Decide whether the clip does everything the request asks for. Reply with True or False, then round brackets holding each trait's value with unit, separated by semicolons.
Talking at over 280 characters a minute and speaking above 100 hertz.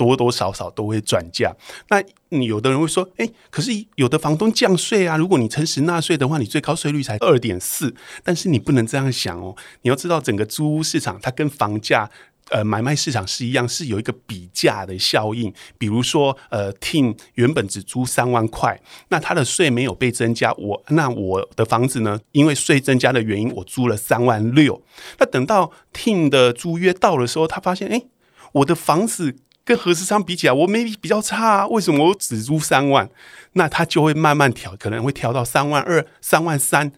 True (300 characters per minute; 140 Hz)